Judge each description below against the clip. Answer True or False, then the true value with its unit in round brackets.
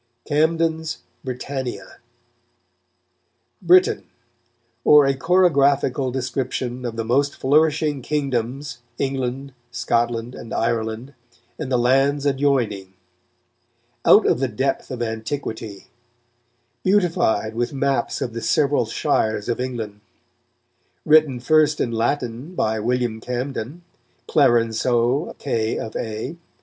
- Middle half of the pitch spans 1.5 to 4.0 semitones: True (3.7 semitones)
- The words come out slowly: True (105 wpm)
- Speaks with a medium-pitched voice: False (130 Hz)